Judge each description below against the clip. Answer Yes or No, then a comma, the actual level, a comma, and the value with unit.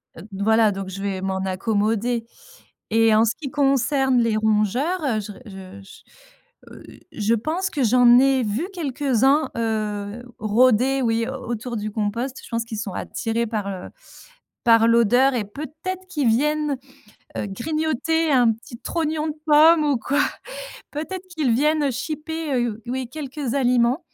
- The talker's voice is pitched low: No, high, 245 Hz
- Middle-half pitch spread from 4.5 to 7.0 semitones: Yes, average, 5.2 semitones